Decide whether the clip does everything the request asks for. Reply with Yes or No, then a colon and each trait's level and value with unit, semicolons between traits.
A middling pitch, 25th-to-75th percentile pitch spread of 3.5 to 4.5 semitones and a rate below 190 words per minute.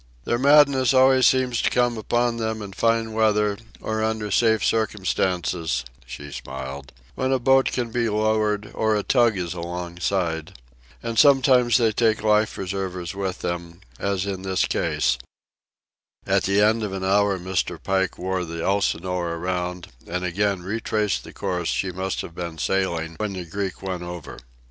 No: low, 100 Hz; average, 3.8 semitones; average, 160 wpm